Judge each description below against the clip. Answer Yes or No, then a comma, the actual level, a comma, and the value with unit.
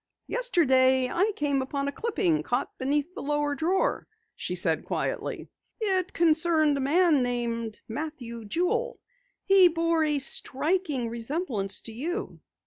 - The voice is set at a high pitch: Yes, very high, 295 Hz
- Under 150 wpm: Yes, slow, 135 wpm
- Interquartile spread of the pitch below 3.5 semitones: No, wide, 5.4 semitones